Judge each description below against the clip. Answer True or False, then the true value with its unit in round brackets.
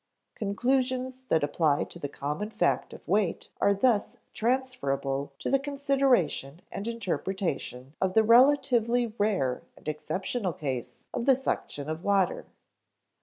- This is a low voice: False (205 Hz)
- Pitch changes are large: True (8.3 semitones)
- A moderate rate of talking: False (130 wpm)